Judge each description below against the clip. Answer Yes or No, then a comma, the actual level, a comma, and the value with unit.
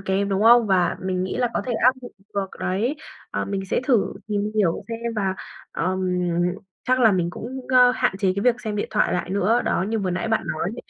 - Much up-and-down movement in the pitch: No, average, 3.7 semitones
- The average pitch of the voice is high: Yes, high, 205 Hz